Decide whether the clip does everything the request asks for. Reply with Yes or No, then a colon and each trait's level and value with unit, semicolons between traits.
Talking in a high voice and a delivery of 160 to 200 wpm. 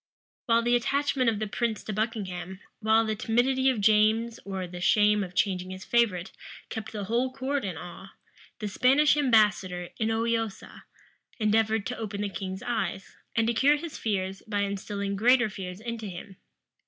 Yes: high, 215 Hz; average, 170 wpm